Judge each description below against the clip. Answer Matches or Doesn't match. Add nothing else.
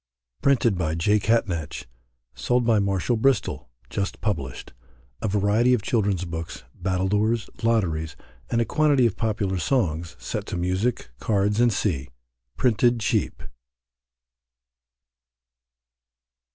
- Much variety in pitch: Doesn't match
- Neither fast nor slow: Doesn't match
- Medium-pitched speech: Doesn't match